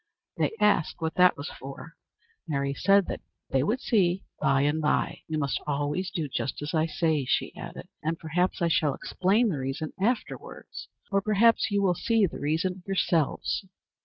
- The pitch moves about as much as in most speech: Yes, average, 4.8 semitones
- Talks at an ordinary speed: Yes, average, 185 wpm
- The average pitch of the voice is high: No, medium, 165 Hz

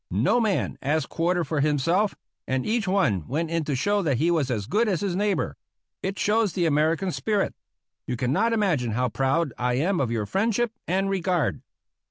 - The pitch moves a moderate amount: No, wide, 6.7 semitones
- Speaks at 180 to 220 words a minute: Yes, average, 190 wpm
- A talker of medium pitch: Yes, medium, 170 Hz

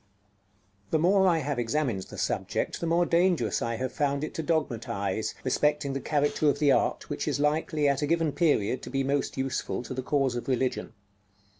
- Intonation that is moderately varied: Yes, average, 3.3 semitones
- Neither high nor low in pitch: Yes, medium, 145 Hz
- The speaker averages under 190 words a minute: No, average, 195 wpm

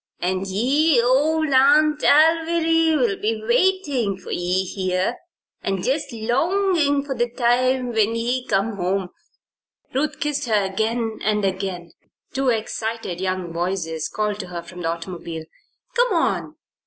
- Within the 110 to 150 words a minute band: Yes, slow, 135 wpm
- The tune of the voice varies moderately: No, wide, 7.0 semitones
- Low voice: No, high, 230 Hz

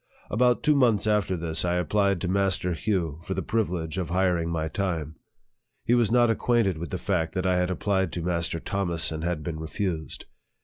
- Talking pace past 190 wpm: Yes, fast, 205 wpm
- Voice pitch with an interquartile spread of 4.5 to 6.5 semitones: No, average, 3.3 semitones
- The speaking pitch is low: Yes, very low, 90 Hz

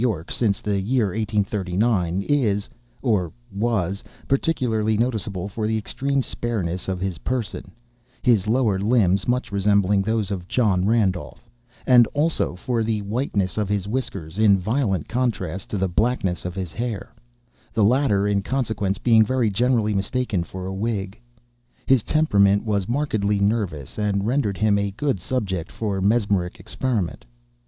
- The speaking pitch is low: Yes, low, 105 Hz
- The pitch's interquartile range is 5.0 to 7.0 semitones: No, average, 3.6 semitones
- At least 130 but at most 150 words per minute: Yes, average, 145 wpm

